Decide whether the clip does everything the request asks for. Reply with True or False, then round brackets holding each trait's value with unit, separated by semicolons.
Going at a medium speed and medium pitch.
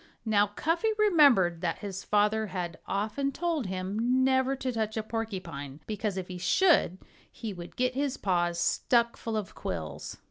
False (165 wpm; 215 Hz)